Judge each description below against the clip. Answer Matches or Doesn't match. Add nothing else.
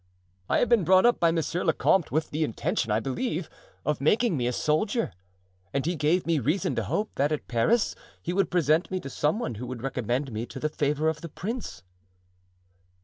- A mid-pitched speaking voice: Matches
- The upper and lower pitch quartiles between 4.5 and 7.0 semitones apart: Matches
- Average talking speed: Doesn't match